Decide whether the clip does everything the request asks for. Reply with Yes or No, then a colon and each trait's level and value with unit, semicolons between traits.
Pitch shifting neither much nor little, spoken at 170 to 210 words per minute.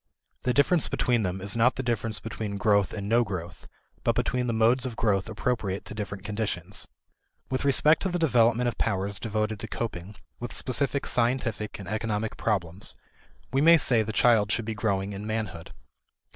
Yes: average, 3.1 semitones; average, 180 wpm